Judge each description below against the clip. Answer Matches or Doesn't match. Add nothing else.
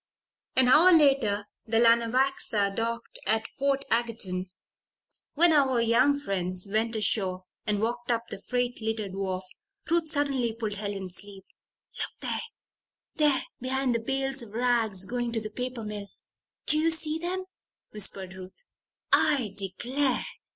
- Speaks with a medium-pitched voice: Doesn't match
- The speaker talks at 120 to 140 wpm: Matches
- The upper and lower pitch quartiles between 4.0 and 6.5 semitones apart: Matches